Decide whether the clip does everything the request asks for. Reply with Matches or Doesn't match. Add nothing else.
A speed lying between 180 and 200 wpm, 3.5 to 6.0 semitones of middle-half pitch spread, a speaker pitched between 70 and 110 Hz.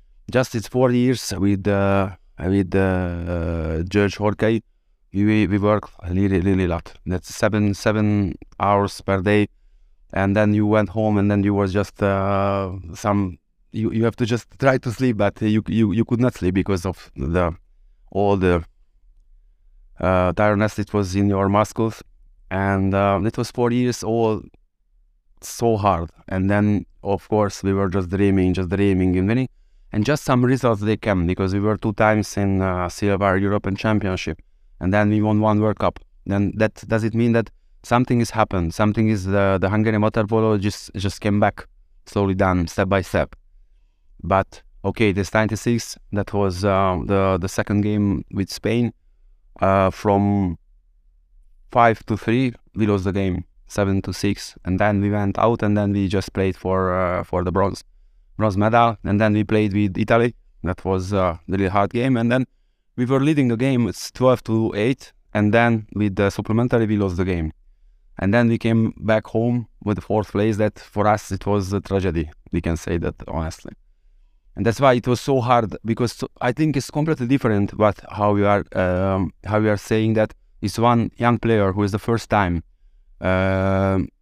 Doesn't match